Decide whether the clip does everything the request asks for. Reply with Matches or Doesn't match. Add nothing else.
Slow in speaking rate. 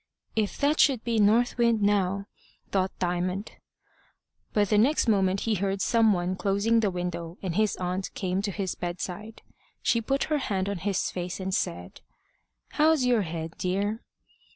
Doesn't match